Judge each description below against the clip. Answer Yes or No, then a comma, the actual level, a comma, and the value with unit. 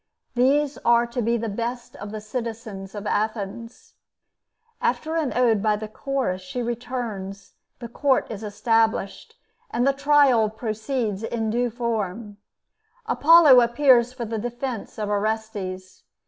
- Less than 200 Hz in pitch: No, high, 230 Hz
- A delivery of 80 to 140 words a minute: Yes, slow, 135 wpm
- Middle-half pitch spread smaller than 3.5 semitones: Yes, average, 2.9 semitones